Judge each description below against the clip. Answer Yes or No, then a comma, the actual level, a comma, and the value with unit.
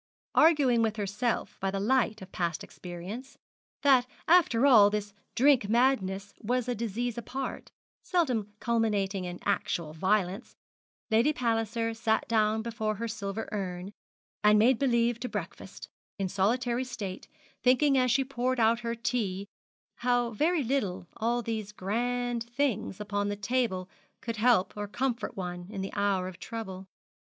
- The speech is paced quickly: No, average, 145 wpm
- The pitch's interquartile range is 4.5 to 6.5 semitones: No, average, 3.6 semitones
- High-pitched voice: Yes, high, 225 Hz